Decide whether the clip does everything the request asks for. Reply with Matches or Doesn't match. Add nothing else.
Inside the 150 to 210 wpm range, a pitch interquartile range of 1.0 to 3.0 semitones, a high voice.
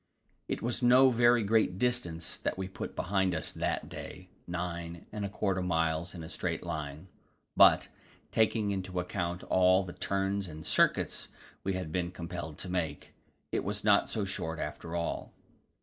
Doesn't match